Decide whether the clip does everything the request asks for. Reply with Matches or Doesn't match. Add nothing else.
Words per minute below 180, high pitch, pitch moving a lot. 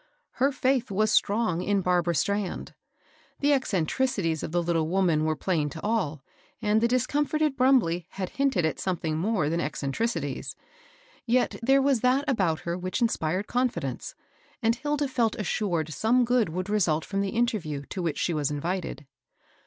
Matches